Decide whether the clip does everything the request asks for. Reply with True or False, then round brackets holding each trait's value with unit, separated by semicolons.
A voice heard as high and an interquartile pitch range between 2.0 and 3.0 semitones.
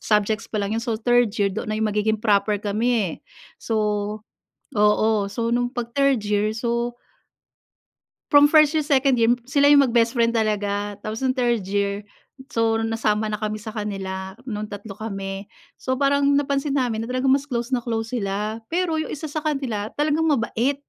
False (225 Hz; 3.8 semitones)